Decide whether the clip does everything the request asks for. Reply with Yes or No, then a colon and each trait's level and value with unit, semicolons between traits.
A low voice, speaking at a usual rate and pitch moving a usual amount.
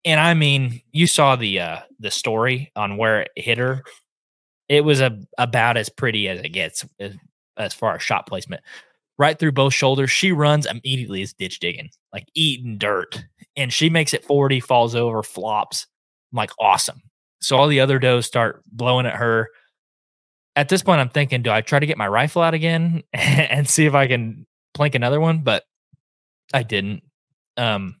Yes: low, 130 Hz; average, 185 wpm; average, 4.5 semitones